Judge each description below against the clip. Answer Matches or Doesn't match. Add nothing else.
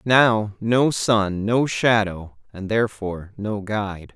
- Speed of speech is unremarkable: Doesn't match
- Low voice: Matches